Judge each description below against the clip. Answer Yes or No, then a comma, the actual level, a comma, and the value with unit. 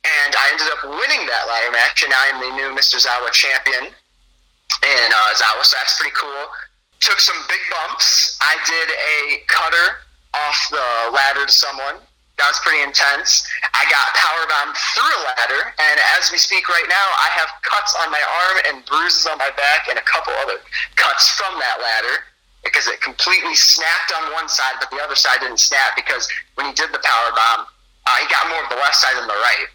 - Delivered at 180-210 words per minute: Yes, fast, 205 wpm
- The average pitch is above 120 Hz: Yes, low, 135 Hz